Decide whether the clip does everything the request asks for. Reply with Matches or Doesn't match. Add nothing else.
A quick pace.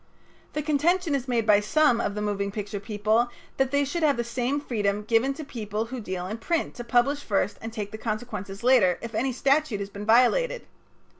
Matches